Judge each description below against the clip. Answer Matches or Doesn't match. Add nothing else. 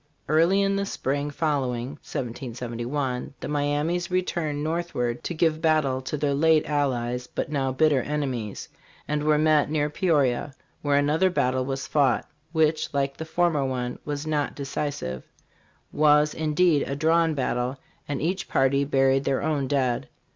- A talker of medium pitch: Matches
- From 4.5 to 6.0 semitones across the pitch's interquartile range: Doesn't match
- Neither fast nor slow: Matches